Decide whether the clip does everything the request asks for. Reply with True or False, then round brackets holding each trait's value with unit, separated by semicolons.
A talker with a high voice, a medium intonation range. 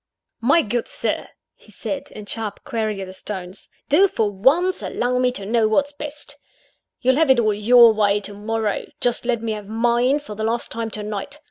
True (230 Hz; 3.6 semitones)